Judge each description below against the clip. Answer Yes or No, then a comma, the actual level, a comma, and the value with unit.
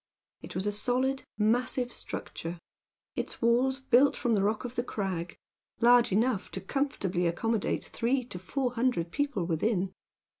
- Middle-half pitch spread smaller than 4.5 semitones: No, average, 4.9 semitones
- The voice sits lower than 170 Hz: No, high, 235 Hz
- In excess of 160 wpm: No, average, 150 wpm